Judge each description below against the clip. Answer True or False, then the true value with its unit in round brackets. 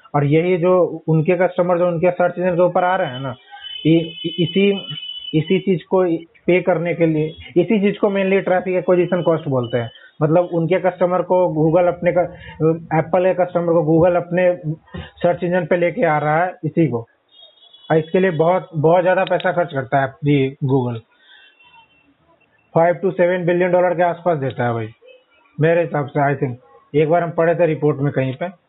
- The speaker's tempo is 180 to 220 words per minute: True (190 wpm)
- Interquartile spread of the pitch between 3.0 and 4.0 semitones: False (2.6 semitones)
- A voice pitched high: False (175 Hz)